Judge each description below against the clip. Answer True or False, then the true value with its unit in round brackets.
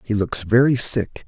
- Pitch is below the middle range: True (110 Hz)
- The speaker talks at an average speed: True (190 wpm)